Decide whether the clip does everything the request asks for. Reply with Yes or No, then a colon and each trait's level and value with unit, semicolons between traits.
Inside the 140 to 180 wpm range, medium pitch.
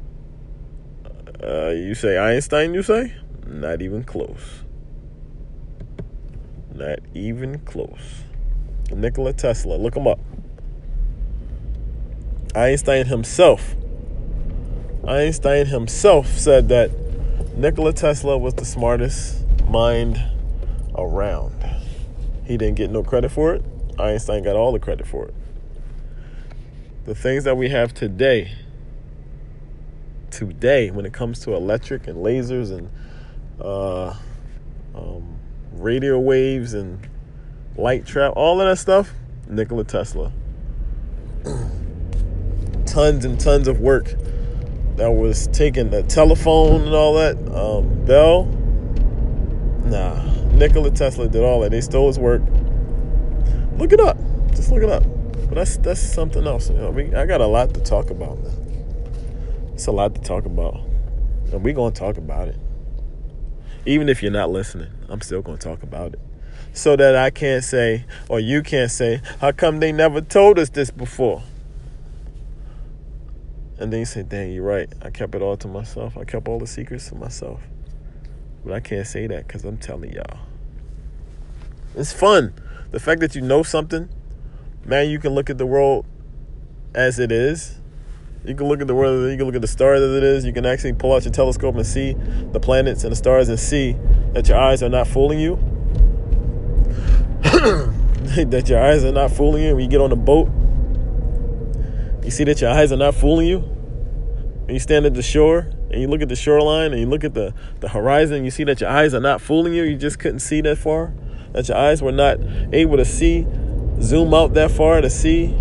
No: average, 165 wpm; low, 125 Hz